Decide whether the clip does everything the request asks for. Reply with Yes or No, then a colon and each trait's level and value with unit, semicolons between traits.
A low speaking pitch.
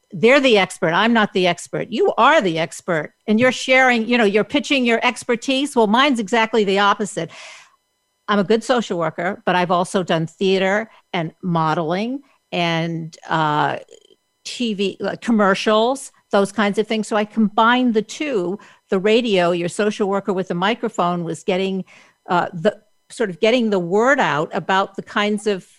No: high, 205 Hz